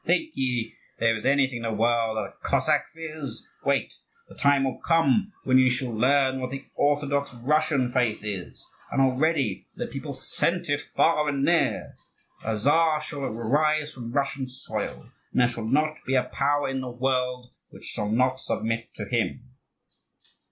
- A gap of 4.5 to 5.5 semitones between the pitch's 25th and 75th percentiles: No, average, 3.4 semitones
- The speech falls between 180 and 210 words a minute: No, average, 170 wpm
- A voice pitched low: Yes, low, 130 Hz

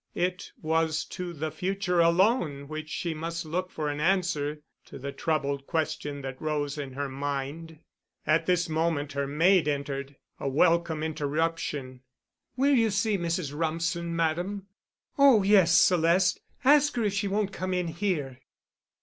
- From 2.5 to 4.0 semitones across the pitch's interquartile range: Yes, average, 3.7 semitones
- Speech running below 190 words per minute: Yes, average, 150 wpm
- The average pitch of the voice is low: No, medium, 165 Hz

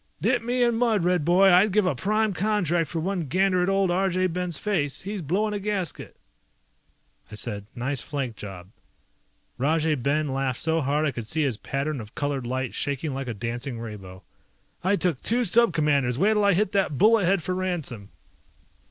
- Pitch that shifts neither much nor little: No, wide, 6.4 semitones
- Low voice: No, medium, 165 Hz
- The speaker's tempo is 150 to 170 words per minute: No, average, 185 wpm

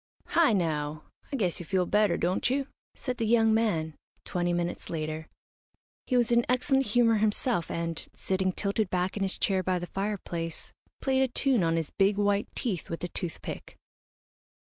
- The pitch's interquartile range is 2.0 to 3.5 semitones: No, average, 4.9 semitones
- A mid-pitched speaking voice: No, high, 195 Hz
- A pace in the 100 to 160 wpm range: No, average, 175 wpm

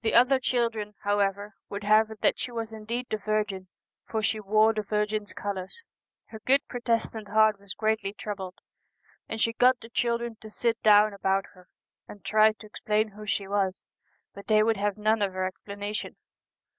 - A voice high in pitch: Yes, high, 215 Hz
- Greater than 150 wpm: Yes, average, 180 wpm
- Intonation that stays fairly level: Yes, narrow, 1.6 semitones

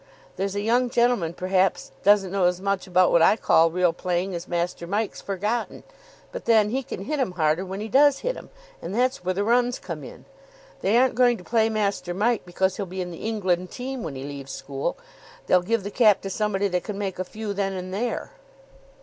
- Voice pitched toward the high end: Yes, high, 195 Hz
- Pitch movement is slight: No, average, 3.9 semitones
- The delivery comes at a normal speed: No, fast, 220 wpm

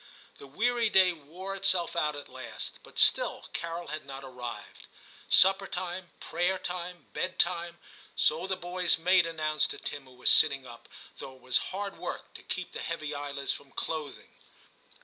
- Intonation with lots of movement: No, average, 4.5 semitones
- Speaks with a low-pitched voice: No, medium, 165 Hz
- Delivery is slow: No, average, 170 wpm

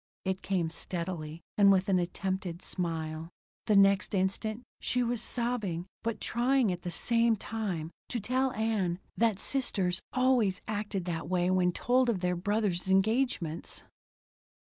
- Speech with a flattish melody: No, average, 4.3 semitones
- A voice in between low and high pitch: No, high, 195 Hz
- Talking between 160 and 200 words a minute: No, average, 140 wpm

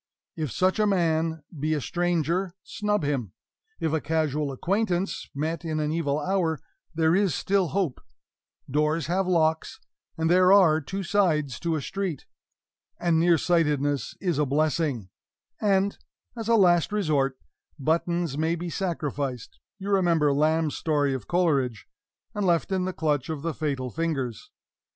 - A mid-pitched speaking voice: Yes, medium, 160 Hz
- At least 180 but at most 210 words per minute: No, average, 150 wpm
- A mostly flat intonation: No, average, 3.5 semitones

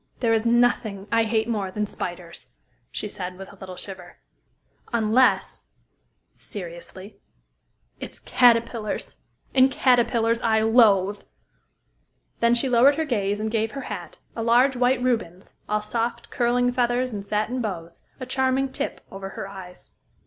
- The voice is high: Yes, high, 225 Hz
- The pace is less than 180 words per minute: Yes, average, 140 wpm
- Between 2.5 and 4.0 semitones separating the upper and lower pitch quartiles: Yes, average, 3.6 semitones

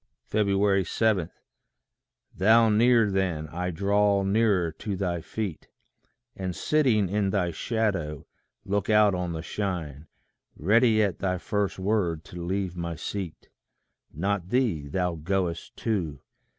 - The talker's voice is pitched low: Yes, very low, 95 Hz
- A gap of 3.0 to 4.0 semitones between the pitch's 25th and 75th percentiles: Yes, average, 3.3 semitones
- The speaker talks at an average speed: No, slow, 125 wpm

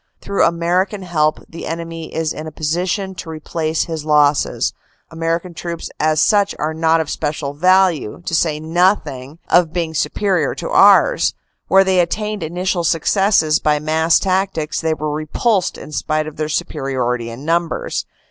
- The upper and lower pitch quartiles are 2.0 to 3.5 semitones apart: Yes, average, 2.8 semitones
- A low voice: No, medium, 165 Hz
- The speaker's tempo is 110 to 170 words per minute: Yes, average, 165 wpm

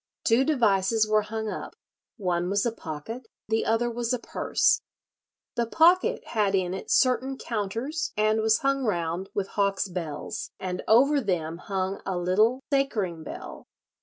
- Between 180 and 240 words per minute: No, average, 155 wpm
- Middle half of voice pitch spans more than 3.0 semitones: Yes, average, 4.2 semitones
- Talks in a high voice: Yes, high, 215 Hz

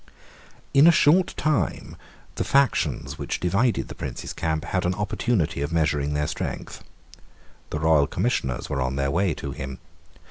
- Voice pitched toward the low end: Yes, very low, 80 Hz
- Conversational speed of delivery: Yes, average, 155 wpm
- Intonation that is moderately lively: No, wide, 7.3 semitones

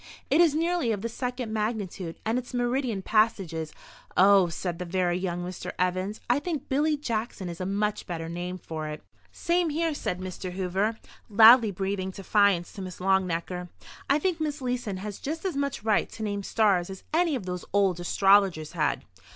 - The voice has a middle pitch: No, high, 200 Hz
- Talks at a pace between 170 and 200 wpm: Yes, average, 185 wpm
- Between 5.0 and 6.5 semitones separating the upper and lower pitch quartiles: Yes, wide, 5.4 semitones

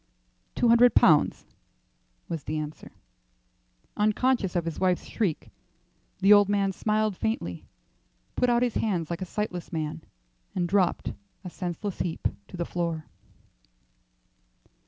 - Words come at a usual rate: No, slow, 130 wpm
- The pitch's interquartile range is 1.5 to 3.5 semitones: No, average, 4.0 semitones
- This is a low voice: No, medium, 185 Hz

